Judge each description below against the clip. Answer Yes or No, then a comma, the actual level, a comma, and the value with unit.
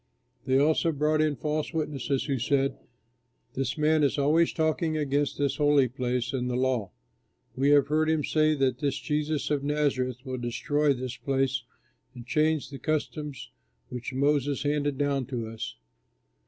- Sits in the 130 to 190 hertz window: Yes, medium, 140 Hz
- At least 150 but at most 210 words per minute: Yes, average, 160 wpm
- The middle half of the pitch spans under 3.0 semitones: Yes, narrow, 2.6 semitones